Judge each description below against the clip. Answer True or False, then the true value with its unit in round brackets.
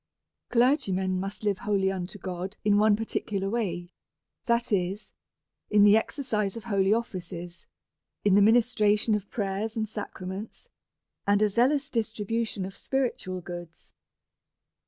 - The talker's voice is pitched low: False (205 Hz)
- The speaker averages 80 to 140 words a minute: True (135 wpm)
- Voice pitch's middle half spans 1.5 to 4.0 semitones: True (2.8 semitones)